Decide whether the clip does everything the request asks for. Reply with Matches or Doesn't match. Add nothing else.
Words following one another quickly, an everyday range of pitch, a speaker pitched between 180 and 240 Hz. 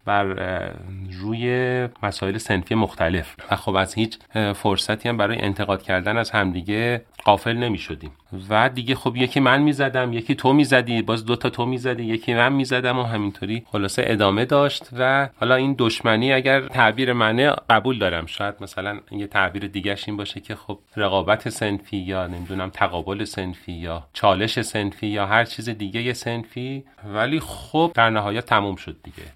Doesn't match